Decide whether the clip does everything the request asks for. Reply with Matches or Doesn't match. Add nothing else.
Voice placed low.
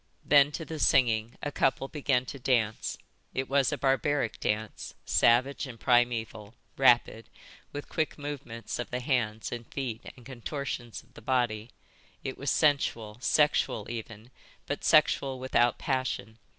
Matches